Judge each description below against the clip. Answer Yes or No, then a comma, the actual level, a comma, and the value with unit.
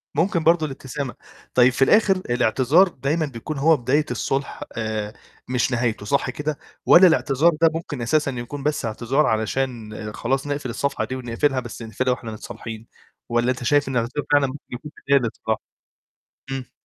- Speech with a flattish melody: No, average, 3.8 semitones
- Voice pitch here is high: No, low, 130 Hz